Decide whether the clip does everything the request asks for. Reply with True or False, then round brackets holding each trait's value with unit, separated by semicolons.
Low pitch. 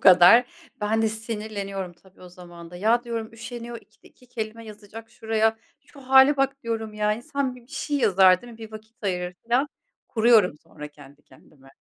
False (220 Hz)